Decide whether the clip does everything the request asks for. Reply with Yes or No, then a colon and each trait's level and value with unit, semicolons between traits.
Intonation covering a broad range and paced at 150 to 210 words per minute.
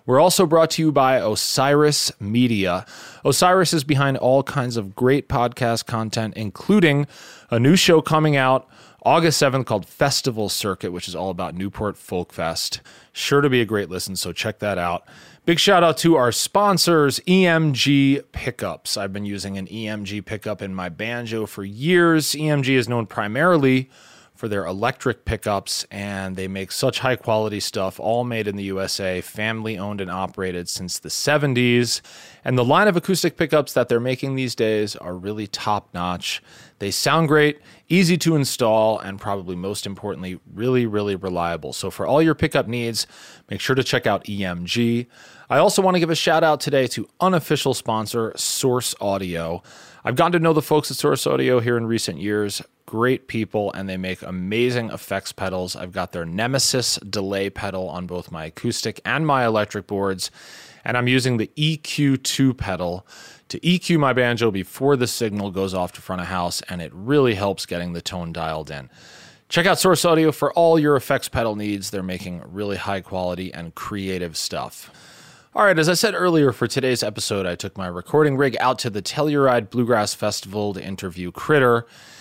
Yes: wide, 6.2 semitones; average, 180 wpm